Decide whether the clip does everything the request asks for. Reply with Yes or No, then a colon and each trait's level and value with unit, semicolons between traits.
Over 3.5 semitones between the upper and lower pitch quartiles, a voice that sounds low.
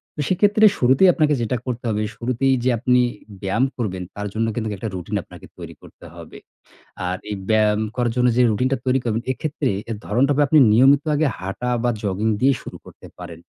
Yes: average, 4.1 semitones; low, 120 Hz